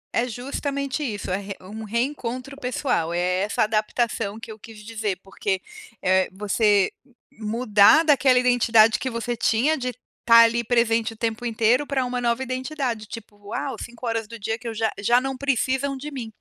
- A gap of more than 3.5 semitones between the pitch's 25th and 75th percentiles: No, average, 3.0 semitones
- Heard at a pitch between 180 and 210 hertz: No, high, 230 Hz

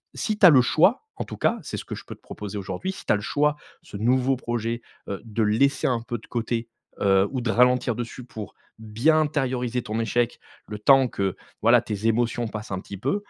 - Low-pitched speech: Yes, low, 120 Hz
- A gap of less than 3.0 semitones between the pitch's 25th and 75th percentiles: No, average, 3.3 semitones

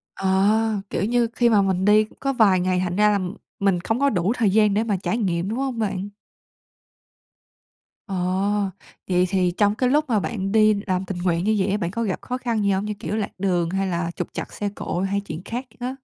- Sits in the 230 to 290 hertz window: No, high, 200 Hz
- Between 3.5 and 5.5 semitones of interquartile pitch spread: No, average, 2.9 semitones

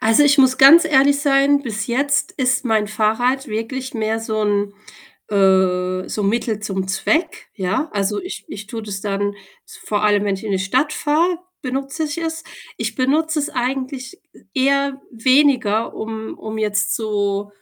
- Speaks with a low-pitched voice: No, high, 230 Hz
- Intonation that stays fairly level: No, average, 5.1 semitones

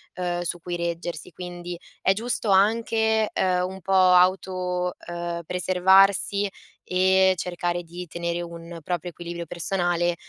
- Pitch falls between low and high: Yes, medium, 180 Hz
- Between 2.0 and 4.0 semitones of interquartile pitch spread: No, narrow, 1.6 semitones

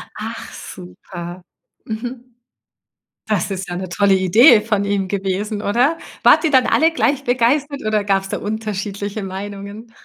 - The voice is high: Yes, high, 205 Hz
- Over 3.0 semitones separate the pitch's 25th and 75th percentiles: Yes, average, 3.6 semitones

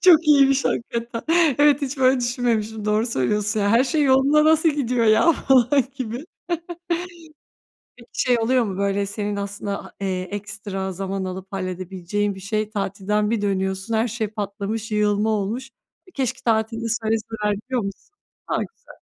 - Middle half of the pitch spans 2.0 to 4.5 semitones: Yes, average, 3.8 semitones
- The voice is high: Yes, high, 220 Hz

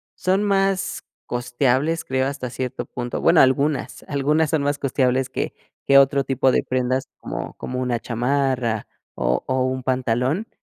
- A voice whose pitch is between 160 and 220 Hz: No, low, 130 Hz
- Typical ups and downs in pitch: No, narrow, 2.1 semitones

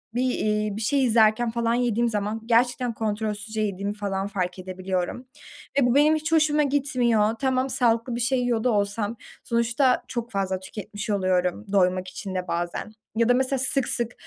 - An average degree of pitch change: Yes, average, 3.5 semitones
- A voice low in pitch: No, high, 225 Hz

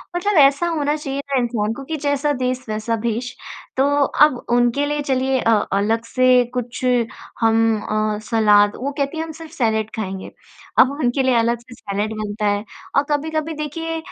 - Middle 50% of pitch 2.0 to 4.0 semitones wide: No, average, 4.4 semitones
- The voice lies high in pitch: Yes, very high, 255 Hz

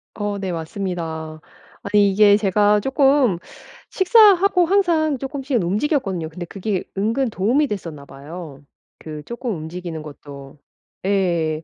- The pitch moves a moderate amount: No, wide, 8.3 semitones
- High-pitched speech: Yes, high, 195 Hz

